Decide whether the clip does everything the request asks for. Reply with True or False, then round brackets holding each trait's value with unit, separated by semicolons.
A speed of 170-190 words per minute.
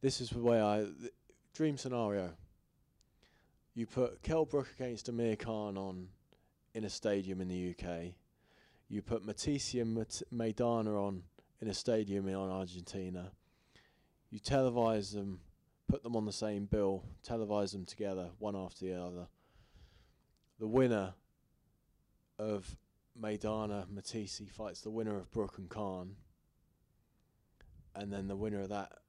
False (140 wpm)